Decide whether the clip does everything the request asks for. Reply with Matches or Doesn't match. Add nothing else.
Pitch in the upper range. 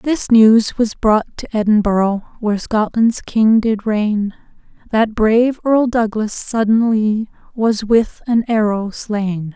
Matches